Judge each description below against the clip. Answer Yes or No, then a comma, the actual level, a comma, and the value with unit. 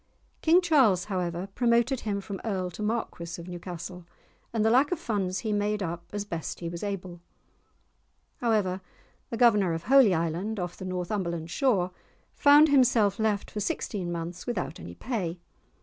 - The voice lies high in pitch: Yes, high, 200 Hz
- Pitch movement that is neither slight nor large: Yes, average, 4.4 semitones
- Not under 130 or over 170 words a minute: Yes, average, 165 wpm